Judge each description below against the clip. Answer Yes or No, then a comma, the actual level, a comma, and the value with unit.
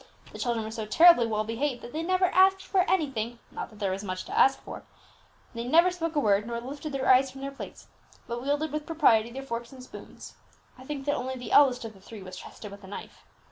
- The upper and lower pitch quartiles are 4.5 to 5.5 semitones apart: Yes, average, 4.8 semitones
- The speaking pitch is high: Yes, very high, 255 Hz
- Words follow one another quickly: Yes, fast, 245 wpm